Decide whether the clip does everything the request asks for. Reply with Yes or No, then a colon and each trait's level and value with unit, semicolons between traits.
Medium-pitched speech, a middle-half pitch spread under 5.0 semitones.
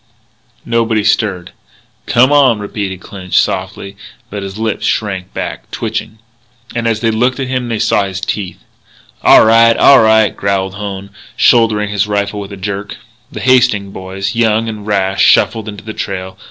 No: low, 105 Hz; narrow, 2.6 semitones